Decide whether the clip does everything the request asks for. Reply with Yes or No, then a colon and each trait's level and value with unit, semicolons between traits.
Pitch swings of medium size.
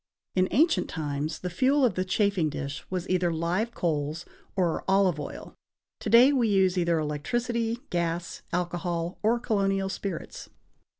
Yes: average, 4.4 semitones